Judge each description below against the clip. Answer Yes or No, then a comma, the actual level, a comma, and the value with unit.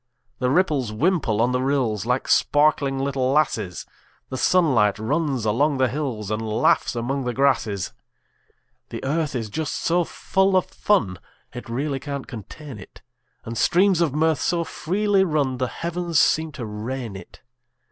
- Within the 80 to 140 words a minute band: No, average, 155 wpm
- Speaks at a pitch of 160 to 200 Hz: No, low, 135 Hz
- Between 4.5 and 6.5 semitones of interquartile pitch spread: Yes, average, 5.3 semitones